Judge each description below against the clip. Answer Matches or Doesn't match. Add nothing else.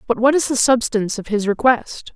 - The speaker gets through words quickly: Matches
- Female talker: Matches